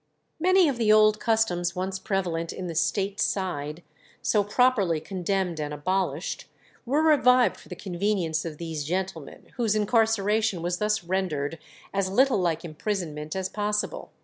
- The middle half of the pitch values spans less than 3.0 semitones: No, average, 4.2 semitones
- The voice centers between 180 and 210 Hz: Yes, high, 190 Hz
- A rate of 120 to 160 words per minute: Yes, average, 150 wpm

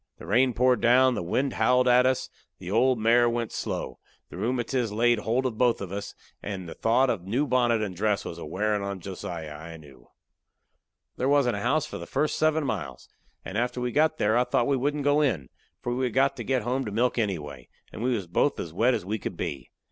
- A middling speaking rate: No, fast, 235 wpm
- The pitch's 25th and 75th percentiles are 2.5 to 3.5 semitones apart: No, average, 4.5 semitones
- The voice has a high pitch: No, low, 120 Hz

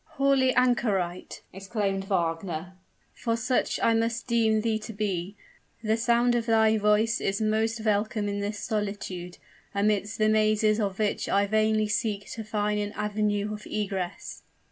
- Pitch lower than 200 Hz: No, high, 215 Hz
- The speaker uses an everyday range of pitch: No, narrow, 1.8 semitones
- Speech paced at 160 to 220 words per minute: No, average, 150 wpm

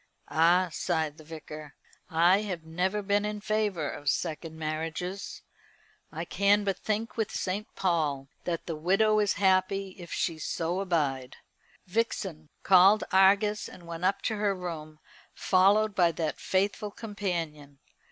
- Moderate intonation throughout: Yes, average, 4.0 semitones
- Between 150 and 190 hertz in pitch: Yes, medium, 185 Hz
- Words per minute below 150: Yes, average, 140 wpm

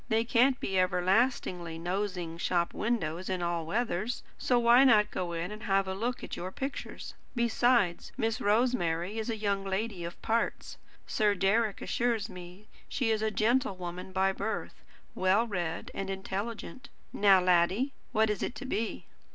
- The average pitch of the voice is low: No, high, 205 Hz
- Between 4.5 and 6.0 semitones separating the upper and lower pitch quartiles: No, average, 4.1 semitones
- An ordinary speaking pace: Yes, average, 160 wpm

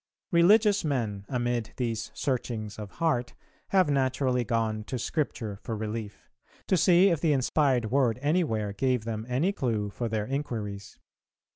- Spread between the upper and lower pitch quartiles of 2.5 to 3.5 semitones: No, average, 5.0 semitones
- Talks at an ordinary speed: Yes, average, 145 wpm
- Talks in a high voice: No, low, 125 Hz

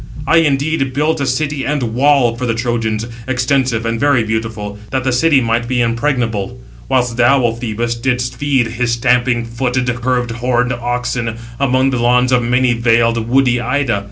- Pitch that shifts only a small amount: Yes, narrow, 2.1 semitones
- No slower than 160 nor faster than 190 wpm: Yes, average, 170 wpm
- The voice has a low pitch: Yes, low, 125 Hz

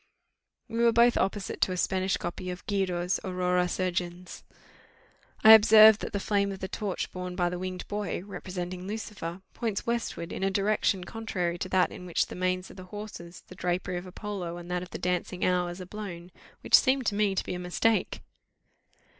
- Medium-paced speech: Yes, average, 195 wpm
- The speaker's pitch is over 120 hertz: Yes, medium, 185 Hz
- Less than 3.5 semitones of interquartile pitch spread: Yes, narrow, 2.4 semitones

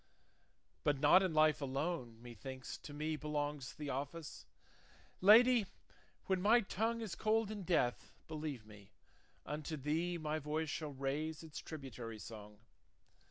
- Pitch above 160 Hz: No, medium, 150 Hz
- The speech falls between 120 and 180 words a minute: Yes, slow, 135 wpm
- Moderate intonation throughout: Yes, average, 4.4 semitones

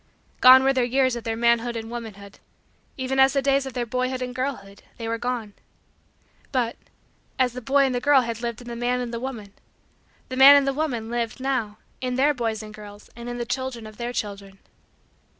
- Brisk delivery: Yes, fast, 215 wpm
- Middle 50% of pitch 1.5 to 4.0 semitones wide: Yes, narrow, 2.5 semitones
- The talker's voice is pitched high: Yes, high, 245 Hz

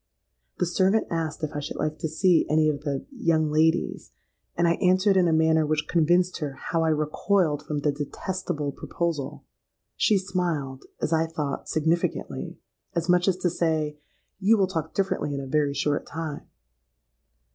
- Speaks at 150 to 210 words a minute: Yes, average, 165 wpm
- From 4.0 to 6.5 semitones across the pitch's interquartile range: No, average, 2.9 semitones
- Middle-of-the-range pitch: Yes, medium, 160 Hz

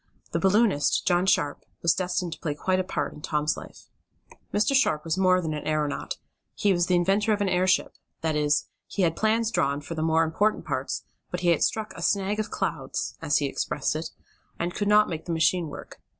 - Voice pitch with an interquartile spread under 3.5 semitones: No, average, 4.1 semitones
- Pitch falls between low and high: Yes, medium, 180 Hz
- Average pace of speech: No, fast, 215 wpm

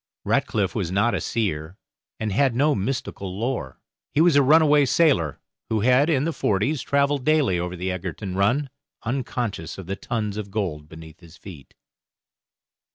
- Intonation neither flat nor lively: No, wide, 7.0 semitones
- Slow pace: No, average, 160 wpm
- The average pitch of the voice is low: Yes, low, 110 Hz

